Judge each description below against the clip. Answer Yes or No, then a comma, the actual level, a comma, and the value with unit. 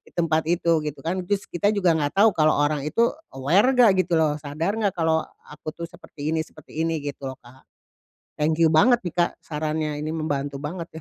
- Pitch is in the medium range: Yes, medium, 160 Hz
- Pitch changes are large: No, narrow, 2.6 semitones